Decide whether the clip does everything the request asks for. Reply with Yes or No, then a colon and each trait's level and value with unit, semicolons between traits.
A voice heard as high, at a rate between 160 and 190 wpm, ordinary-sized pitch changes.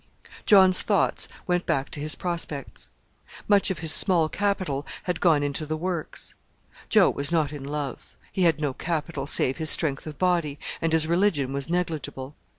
No: medium, 160 Hz; average, 170 wpm; average, 3.6 semitones